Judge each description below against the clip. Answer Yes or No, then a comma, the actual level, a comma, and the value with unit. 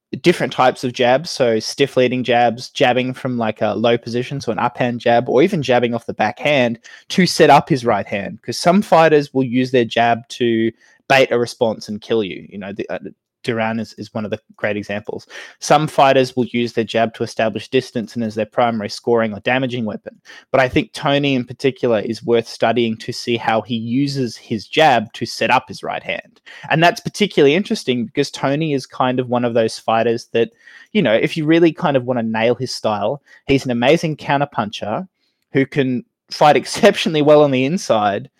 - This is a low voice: Yes, low, 125 Hz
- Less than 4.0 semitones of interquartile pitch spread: Yes, average, 3.2 semitones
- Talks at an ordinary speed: No, fast, 210 wpm